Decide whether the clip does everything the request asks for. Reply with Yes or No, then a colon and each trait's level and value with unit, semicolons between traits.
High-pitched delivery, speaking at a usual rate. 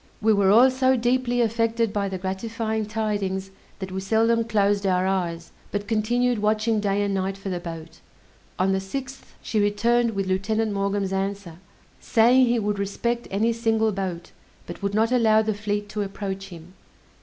Yes: high, 205 Hz; average, 175 wpm